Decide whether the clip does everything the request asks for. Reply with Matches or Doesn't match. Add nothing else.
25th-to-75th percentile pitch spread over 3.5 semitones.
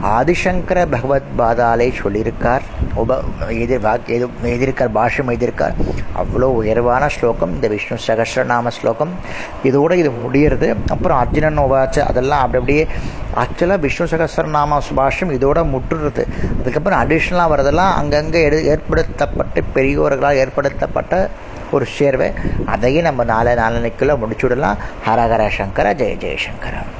Matches